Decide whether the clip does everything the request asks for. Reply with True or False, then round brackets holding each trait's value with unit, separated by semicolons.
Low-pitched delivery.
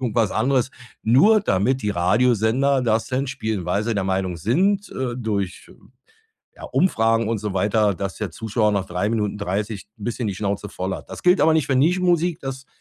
True (110 Hz)